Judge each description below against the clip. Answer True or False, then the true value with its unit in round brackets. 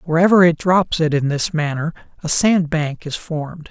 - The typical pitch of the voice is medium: True (160 Hz)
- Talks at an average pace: True (195 wpm)